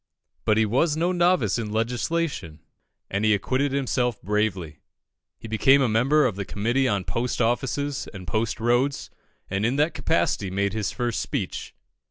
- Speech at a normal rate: Yes, average, 165 wpm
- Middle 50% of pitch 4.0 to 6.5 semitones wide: Yes, average, 4.7 semitones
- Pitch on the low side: Yes, low, 115 Hz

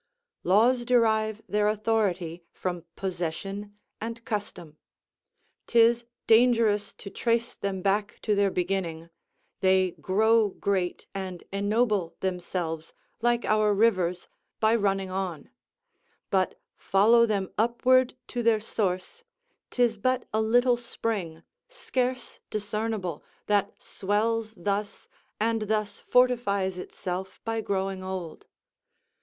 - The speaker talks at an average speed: No, slow, 110 wpm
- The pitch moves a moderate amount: Yes, average, 3.3 semitones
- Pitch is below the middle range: No, high, 205 Hz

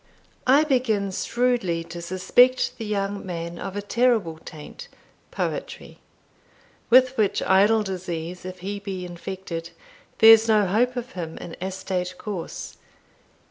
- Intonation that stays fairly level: No, average, 4.0 semitones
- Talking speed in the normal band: No, slow, 130 wpm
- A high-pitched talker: Yes, high, 195 Hz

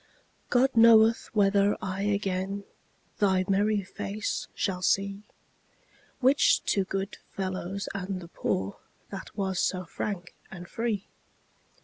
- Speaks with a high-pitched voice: Yes, high, 195 Hz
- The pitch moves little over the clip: Yes, narrow, 1.8 semitones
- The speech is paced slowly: Yes, slow, 115 wpm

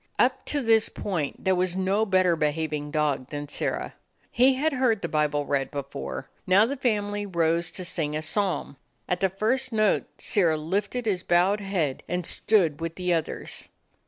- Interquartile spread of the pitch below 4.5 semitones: No, average, 5.1 semitones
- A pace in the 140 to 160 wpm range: No, average, 175 wpm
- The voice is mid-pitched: Yes, medium, 180 Hz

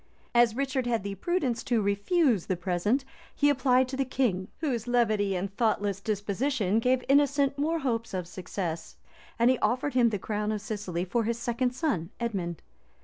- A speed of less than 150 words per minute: No, average, 175 wpm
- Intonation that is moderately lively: Yes, average, 4.6 semitones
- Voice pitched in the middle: No, high, 230 Hz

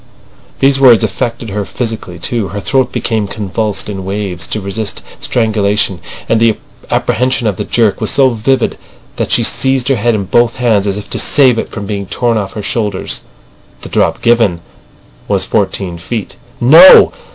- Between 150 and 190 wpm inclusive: Yes, average, 175 wpm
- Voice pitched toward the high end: No, low, 110 Hz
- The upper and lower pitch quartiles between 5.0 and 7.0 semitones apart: No, average, 3.2 semitones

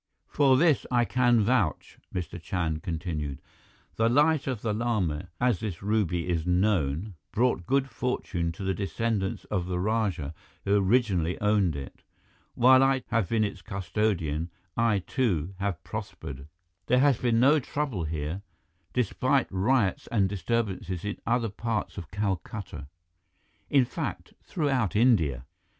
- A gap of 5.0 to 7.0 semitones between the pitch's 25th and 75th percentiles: Yes, wide, 5.4 semitones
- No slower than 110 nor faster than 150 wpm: Yes, average, 140 wpm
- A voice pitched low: Yes, low, 105 Hz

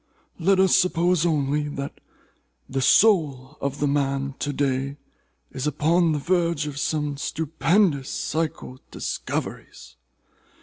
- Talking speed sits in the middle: No, slow, 125 wpm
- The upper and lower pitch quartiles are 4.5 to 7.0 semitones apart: No, average, 3.3 semitones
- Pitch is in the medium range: Yes, medium, 150 Hz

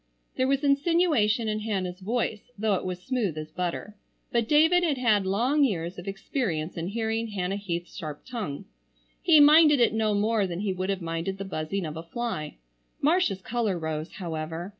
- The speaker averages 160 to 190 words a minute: Yes, average, 180 wpm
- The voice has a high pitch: Yes, high, 205 Hz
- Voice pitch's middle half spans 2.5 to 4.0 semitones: No, wide, 5.4 semitones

